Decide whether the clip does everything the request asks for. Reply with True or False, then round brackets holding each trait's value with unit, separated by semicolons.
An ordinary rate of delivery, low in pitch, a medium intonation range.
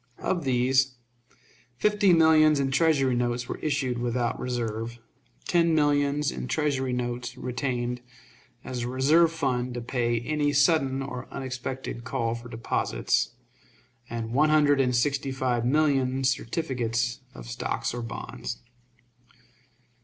False (125 wpm; 130 Hz; 3.1 semitones)